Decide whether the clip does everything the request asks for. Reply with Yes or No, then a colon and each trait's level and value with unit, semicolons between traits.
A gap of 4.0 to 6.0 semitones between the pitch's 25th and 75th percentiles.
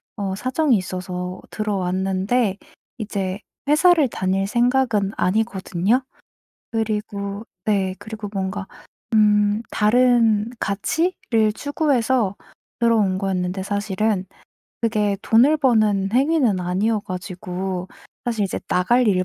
No: average, 3.4 semitones